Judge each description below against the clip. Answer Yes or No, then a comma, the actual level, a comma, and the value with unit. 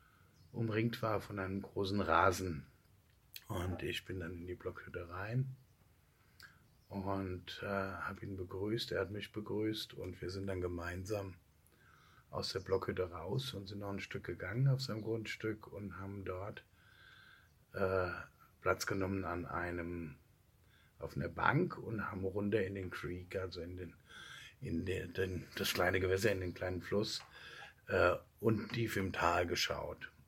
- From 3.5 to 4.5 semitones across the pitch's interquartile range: No, average, 3.1 semitones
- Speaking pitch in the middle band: No, very low, 95 Hz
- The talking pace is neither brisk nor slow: Yes, average, 155 wpm